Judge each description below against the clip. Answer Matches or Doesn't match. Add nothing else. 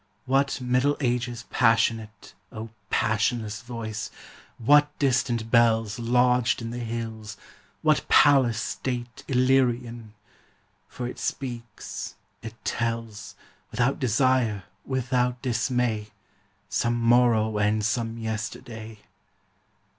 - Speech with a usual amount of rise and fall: Doesn't match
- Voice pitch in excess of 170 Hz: Doesn't match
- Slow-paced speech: Matches